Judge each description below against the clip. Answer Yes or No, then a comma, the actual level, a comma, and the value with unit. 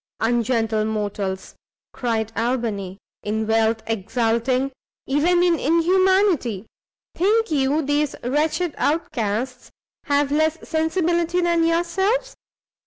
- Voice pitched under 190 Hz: No, very high, 275 Hz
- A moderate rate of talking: No, slow, 95 wpm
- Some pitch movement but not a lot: No, wide, 7.0 semitones